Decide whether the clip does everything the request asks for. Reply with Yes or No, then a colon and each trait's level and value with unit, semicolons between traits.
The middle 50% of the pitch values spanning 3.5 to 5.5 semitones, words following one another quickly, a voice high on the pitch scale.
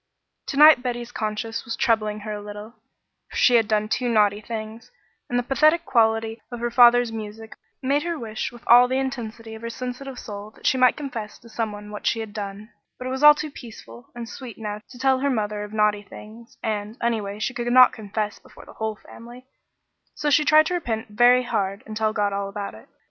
No: average, 2.8 semitones; fast, 220 wpm; high, 225 Hz